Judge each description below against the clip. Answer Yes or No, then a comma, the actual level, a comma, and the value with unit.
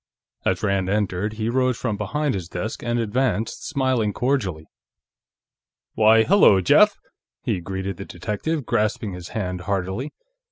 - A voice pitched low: Yes, low, 105 Hz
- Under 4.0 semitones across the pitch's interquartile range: No, average, 4.3 semitones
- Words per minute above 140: No, slow, 135 wpm